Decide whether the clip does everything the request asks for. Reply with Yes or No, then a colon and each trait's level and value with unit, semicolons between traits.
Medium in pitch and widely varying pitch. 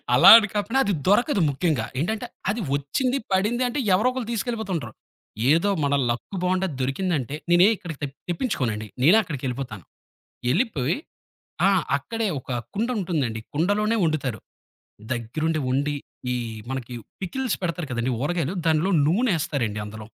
Yes: medium, 165 Hz; wide, 7.3 semitones